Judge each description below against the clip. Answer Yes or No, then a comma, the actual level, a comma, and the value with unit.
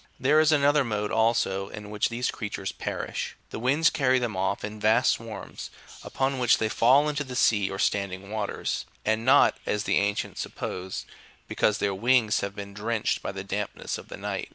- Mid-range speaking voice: No, low, 110 Hz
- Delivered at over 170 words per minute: Yes, average, 200 wpm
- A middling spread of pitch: Yes, average, 4.1 semitones